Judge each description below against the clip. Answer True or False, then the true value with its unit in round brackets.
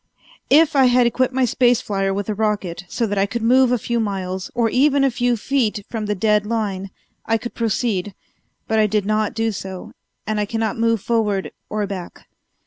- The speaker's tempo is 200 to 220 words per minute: True (205 wpm)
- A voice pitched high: True (220 Hz)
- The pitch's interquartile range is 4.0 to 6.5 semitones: False (3.0 semitones)